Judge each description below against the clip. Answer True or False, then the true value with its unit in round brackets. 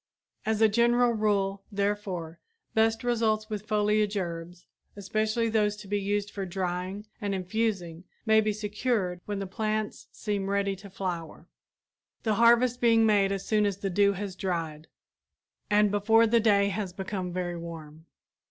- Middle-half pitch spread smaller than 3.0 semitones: True (2.5 semitones)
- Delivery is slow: False (155 wpm)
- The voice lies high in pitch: True (205 Hz)